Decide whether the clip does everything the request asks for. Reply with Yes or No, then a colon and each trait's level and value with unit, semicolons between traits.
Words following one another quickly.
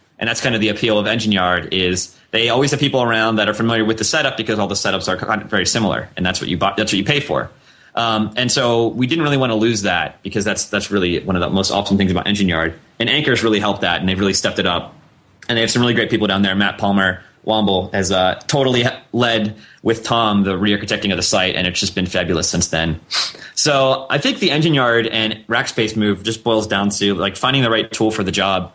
Yes: fast, 255 wpm